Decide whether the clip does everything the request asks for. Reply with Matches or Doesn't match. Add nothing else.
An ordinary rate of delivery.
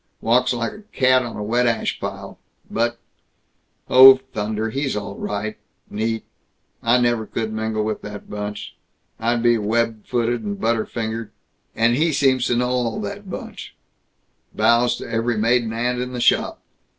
Matches